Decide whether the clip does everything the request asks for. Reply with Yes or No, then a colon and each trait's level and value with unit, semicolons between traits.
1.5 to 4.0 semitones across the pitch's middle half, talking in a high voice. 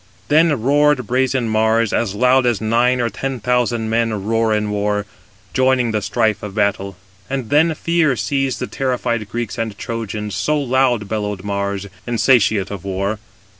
No: average, 3.7 semitones; low, 115 Hz